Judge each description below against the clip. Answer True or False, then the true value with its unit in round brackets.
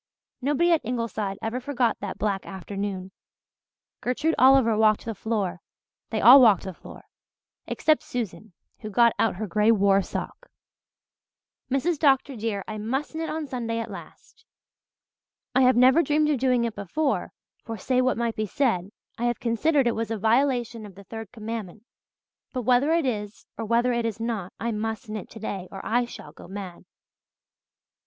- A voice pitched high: True (230 Hz)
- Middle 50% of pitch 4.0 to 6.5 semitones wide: False (3.5 semitones)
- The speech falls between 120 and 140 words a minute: False (170 wpm)